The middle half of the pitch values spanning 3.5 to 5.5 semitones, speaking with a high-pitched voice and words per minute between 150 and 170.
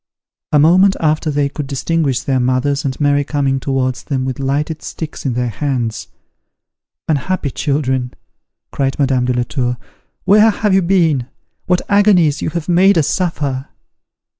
No: average, 4.0 semitones; medium, 145 Hz; average, 155 wpm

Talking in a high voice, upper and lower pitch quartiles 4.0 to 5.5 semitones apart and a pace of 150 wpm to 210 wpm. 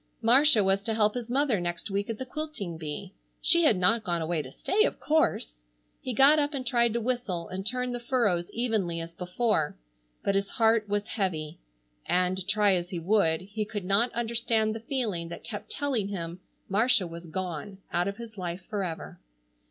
Yes: high, 205 Hz; average, 4.9 semitones; average, 190 wpm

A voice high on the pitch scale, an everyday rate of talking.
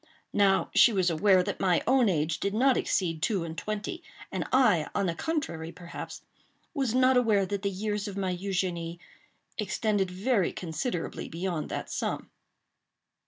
Yes: high, 195 Hz; average, 160 wpm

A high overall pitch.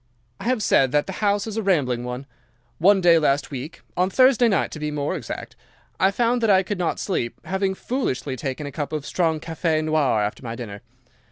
No: medium, 160 Hz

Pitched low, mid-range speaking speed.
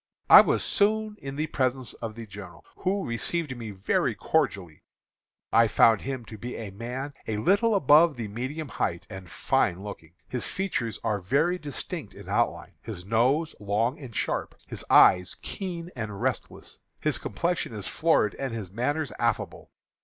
Yes: low, 120 Hz; average, 165 wpm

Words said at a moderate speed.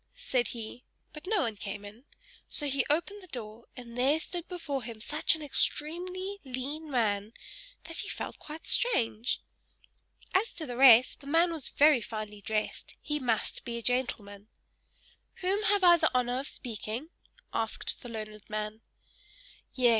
Yes: average, 160 wpm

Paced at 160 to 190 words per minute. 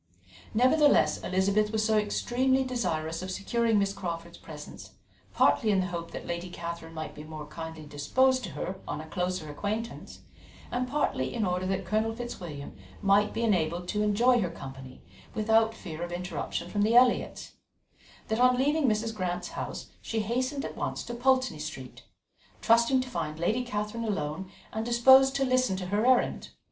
Yes: average, 170 wpm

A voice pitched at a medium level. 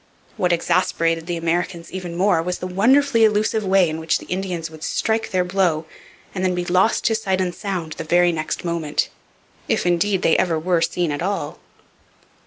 Yes: medium, 180 Hz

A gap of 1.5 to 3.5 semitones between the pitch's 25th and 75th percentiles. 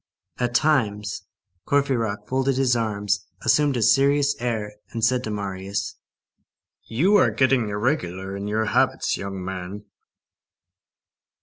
No: average, 4.5 semitones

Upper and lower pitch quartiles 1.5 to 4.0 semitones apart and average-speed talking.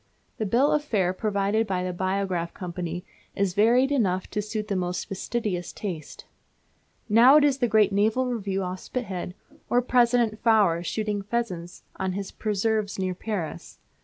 Yes: average, 3.6 semitones; average, 160 wpm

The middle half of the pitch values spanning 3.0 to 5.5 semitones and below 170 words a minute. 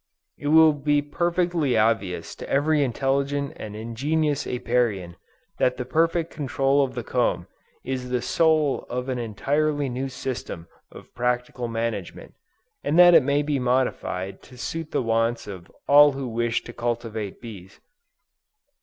Yes: average, 4.1 semitones; average, 145 wpm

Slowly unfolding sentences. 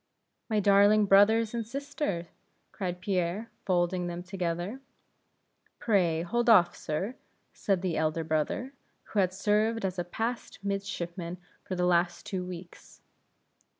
Yes: slow, 130 wpm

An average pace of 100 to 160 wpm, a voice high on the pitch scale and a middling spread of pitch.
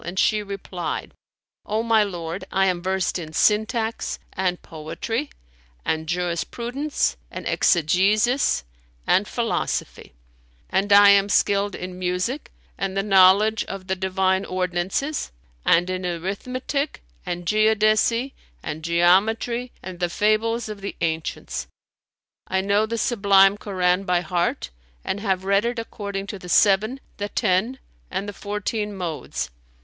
Yes: slow, 135 wpm; high, 195 Hz; average, 3.0 semitones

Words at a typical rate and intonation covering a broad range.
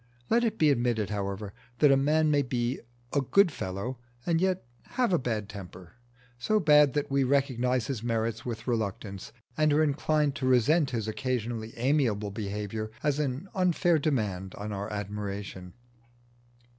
Yes: average, 155 wpm; wide, 5.9 semitones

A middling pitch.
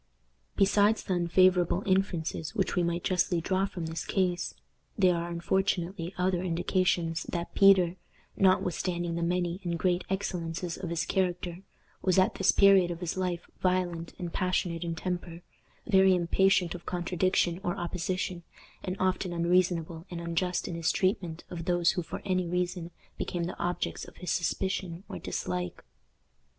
Yes: medium, 180 Hz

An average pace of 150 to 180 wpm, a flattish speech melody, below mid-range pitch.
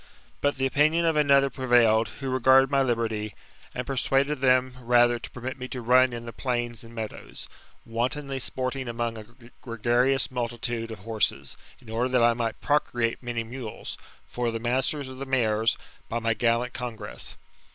Yes: average, 170 wpm; narrow, 2.2 semitones; low, 120 Hz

